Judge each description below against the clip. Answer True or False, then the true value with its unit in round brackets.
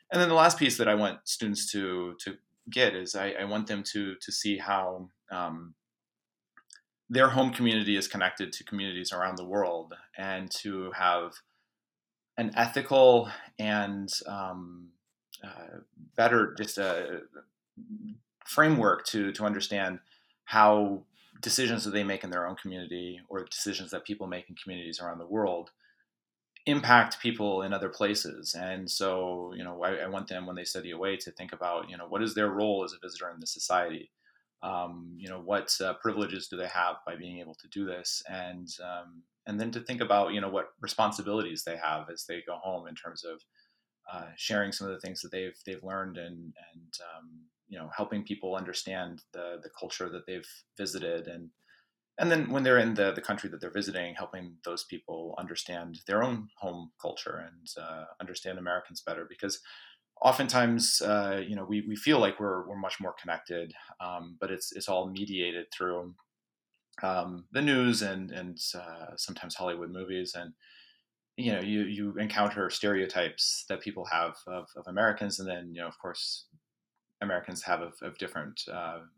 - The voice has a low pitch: True (95 Hz)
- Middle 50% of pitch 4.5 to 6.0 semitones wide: False (2.8 semitones)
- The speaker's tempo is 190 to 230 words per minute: False (180 wpm)